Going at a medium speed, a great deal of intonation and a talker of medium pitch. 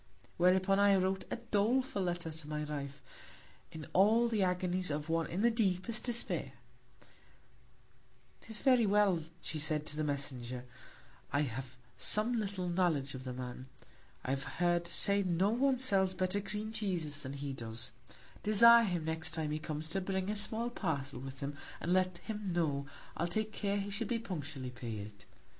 Yes: average, 170 wpm; wide, 5.8 semitones; medium, 180 Hz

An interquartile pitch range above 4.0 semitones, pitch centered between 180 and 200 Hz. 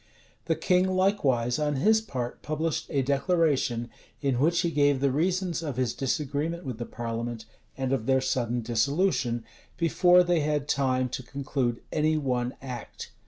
No: average, 4.8 semitones; medium, 140 Hz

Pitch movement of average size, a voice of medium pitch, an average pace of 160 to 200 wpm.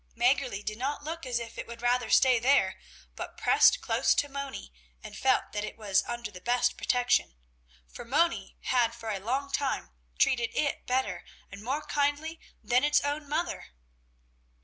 No: average, 3.7 semitones; very high, 250 Hz; average, 170 wpm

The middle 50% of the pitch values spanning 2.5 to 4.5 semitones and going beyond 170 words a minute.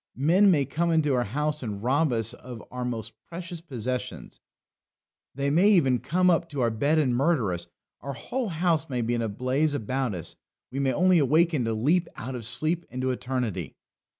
No: average, 5.1 semitones; average, 195 wpm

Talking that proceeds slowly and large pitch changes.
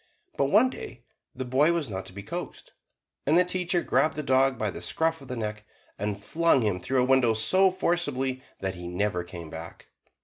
No: fast, 205 wpm; wide, 7.7 semitones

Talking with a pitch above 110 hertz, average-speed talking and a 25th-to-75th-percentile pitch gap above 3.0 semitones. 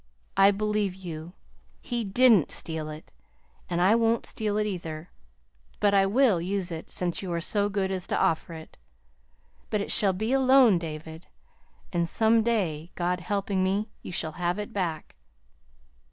Yes: high, 190 Hz; average, 165 wpm; average, 3.8 semitones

